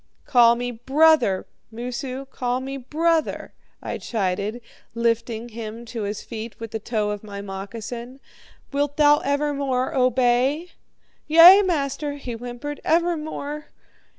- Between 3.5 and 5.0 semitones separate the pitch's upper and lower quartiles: Yes, average, 4.2 semitones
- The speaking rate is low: Yes, slow, 125 wpm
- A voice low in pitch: No, very high, 250 Hz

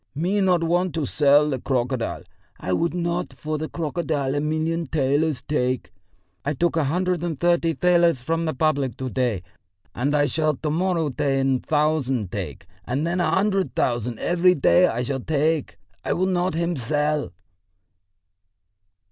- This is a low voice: No, medium, 155 Hz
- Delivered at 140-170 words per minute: Yes, average, 165 wpm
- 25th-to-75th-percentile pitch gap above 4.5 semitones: No, average, 4.2 semitones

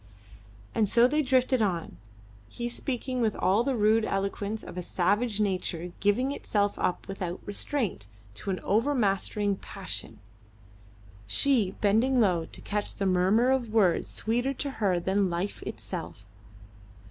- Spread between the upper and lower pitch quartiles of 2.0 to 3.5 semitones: No, average, 4.3 semitones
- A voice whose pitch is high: Yes, high, 205 Hz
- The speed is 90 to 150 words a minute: Yes, average, 140 wpm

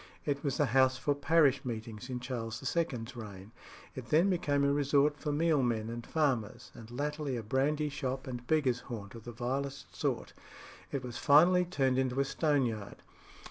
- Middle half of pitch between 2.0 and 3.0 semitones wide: No, average, 3.5 semitones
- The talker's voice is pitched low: Yes, low, 130 Hz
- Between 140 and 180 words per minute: Yes, average, 175 wpm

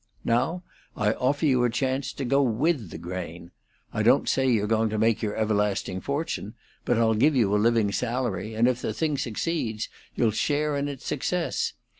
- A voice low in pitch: Yes, low, 115 Hz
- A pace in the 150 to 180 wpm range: No, average, 190 wpm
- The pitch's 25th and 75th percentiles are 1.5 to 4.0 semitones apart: No, average, 4.5 semitones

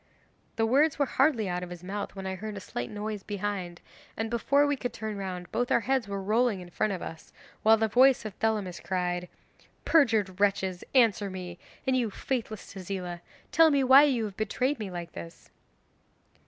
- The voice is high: Yes, high, 205 Hz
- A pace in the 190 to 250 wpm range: Yes, average, 195 wpm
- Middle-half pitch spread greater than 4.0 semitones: Yes, average, 4.6 semitones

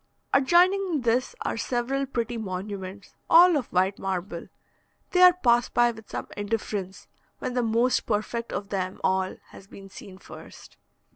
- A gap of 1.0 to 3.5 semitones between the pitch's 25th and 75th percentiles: No, average, 4.9 semitones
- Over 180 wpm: No, average, 150 wpm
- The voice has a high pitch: Yes, high, 225 Hz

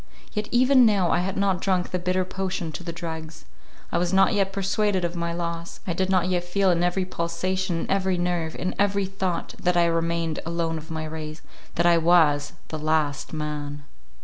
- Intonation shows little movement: Yes, narrow, 2.3 semitones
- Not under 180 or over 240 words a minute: Yes, average, 200 wpm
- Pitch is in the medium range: Yes, medium, 175 Hz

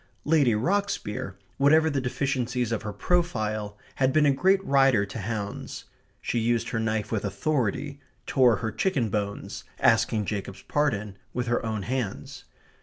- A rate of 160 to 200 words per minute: No, average, 150 wpm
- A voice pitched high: No, low, 120 Hz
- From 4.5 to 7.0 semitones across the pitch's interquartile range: Yes, average, 4.8 semitones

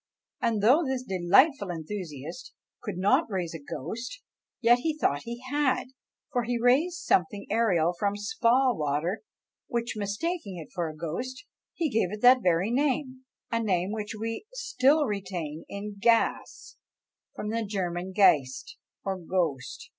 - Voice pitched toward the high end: Yes, high, 210 Hz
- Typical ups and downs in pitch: No, wide, 6.1 semitones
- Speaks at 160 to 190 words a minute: No, average, 145 wpm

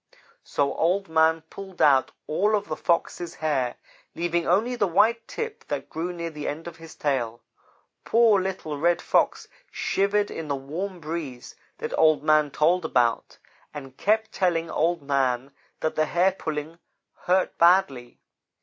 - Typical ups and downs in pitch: Yes, average, 4.1 semitones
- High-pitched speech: No, medium, 165 Hz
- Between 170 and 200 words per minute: No, average, 155 wpm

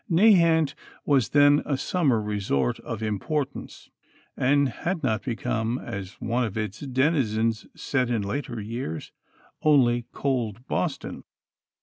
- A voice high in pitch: No, low, 125 Hz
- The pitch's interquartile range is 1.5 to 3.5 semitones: No, average, 4.8 semitones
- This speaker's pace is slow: Yes, slow, 120 wpm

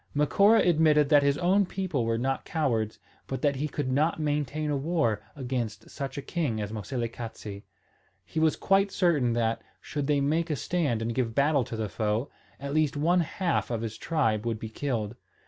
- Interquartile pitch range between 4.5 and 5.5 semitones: Yes, average, 5.2 semitones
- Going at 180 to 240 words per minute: Yes, average, 190 wpm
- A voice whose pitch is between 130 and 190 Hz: Yes, medium, 140 Hz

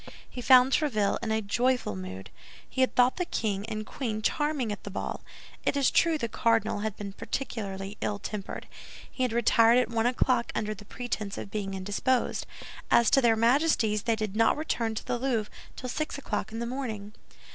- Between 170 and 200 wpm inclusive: Yes, average, 195 wpm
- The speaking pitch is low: No, high, 225 Hz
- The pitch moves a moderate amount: Yes, average, 3.3 semitones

